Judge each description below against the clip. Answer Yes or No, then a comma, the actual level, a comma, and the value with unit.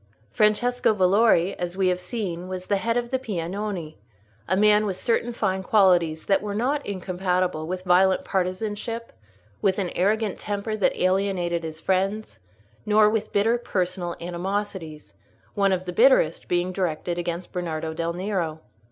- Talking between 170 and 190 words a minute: No, average, 150 wpm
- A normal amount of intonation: Yes, average, 3.1 semitones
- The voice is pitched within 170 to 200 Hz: Yes, high, 190 Hz